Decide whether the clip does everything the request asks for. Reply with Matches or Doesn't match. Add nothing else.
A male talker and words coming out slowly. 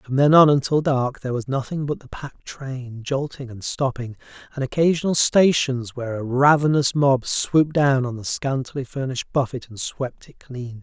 Doesn't match